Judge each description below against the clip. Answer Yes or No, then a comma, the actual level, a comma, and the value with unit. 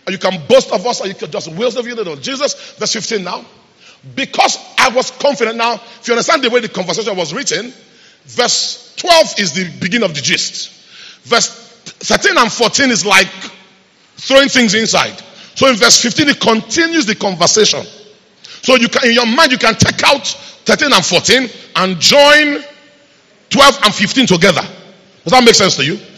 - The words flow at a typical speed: Yes, average, 185 wpm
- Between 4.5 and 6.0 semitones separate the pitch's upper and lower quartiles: Yes, average, 4.8 semitones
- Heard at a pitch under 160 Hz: No, high, 230 Hz